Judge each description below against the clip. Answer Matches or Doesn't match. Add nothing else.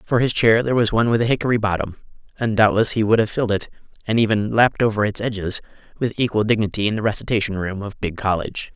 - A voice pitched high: Doesn't match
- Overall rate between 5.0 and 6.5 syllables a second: Doesn't match